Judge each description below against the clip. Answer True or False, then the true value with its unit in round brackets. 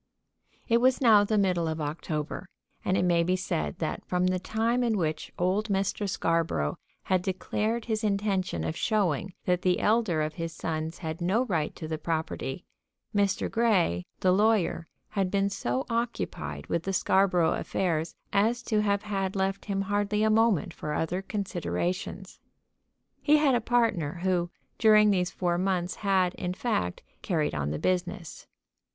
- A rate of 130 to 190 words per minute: True (165 wpm)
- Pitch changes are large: False (4.0 semitones)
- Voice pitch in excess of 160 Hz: True (185 Hz)